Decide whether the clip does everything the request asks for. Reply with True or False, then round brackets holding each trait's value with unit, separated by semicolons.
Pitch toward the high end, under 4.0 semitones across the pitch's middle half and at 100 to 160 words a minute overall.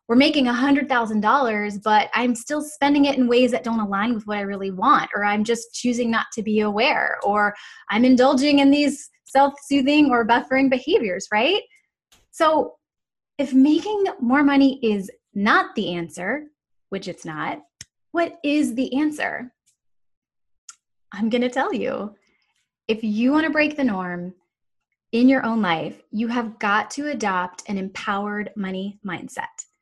False (245 Hz; 5.3 semitones; 155 wpm)